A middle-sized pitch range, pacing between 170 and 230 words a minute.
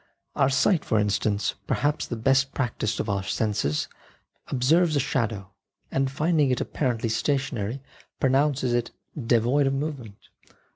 No: average, 4.2 semitones; average, 140 wpm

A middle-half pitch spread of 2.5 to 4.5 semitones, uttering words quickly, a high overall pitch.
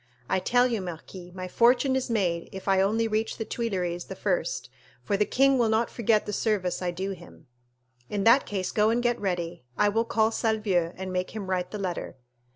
Yes: average, 3.8 semitones; fast, 210 wpm; high, 205 Hz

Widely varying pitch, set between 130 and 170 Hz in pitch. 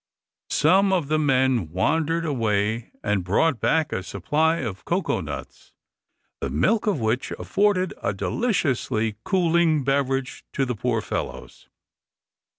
Yes: wide, 7.0 semitones; low, 135 Hz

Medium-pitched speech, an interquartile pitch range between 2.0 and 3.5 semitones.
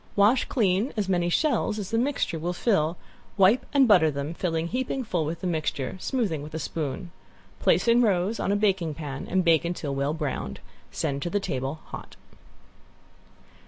No: medium, 175 Hz; average, 5.1 semitones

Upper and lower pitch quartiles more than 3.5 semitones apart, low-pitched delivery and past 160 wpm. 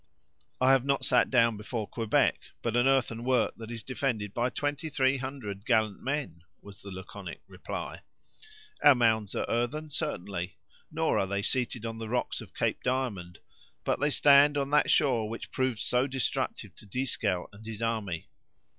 Yes: average, 4.0 semitones; low, 120 Hz; average, 170 wpm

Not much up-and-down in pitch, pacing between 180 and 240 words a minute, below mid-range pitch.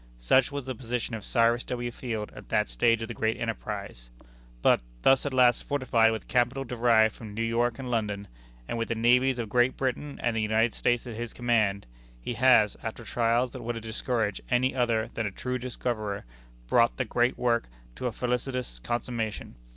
Yes: narrow, 1.9 semitones; average, 195 wpm; low, 120 Hz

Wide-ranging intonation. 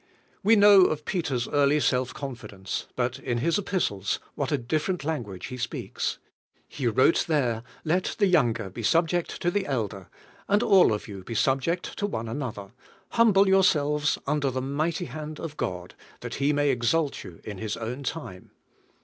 Yes: wide, 6.1 semitones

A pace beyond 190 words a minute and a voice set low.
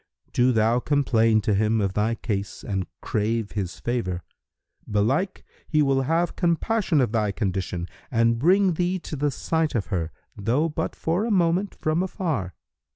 No: average, 160 wpm; low, 120 Hz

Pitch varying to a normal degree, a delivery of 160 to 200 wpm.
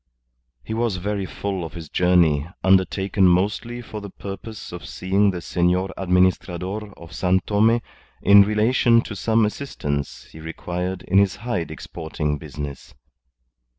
No: average, 3.2 semitones; average, 140 wpm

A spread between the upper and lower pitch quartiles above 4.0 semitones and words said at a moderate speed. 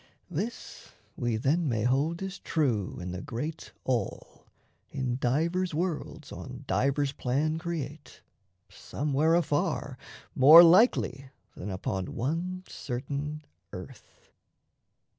No: average, 4.9 semitones; slow, 105 wpm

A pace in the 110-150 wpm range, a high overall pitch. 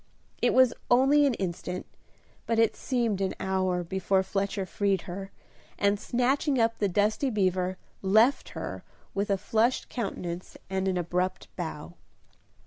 Yes: average, 140 wpm; high, 195 Hz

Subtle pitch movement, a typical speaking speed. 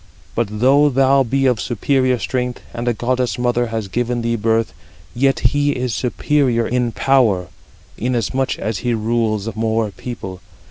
Yes: narrow, 2.3 semitones; average, 150 wpm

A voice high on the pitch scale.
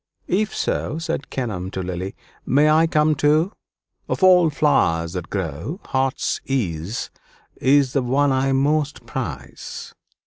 No: low, 135 Hz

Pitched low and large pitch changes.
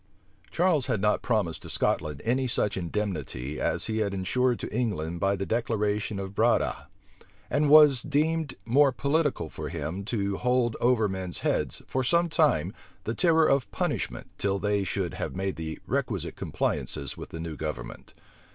Yes: low, 105 Hz; wide, 5.7 semitones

